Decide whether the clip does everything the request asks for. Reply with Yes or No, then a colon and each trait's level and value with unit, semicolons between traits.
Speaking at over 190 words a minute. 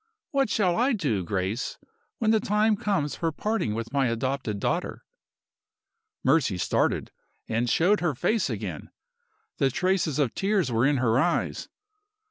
No: average, 145 wpm